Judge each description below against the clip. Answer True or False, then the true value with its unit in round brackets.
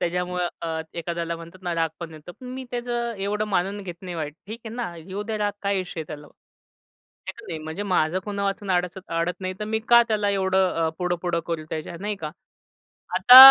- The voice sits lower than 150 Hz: False (185 Hz)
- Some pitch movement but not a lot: True (3.5 semitones)